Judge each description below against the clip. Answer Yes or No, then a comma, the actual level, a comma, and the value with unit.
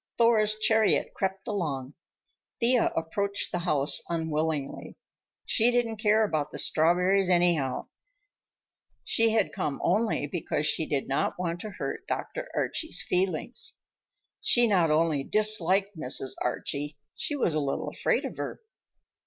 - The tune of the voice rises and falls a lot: Yes, wide, 5.7 semitones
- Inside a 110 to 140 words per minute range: Yes, slow, 135 wpm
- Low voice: No, medium, 180 Hz